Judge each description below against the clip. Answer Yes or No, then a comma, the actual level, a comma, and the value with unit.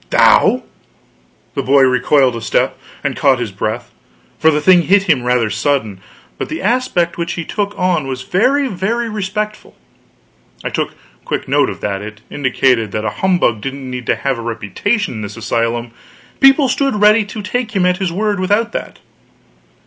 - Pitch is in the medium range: Yes, medium, 160 Hz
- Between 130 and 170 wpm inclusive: No, average, 180 wpm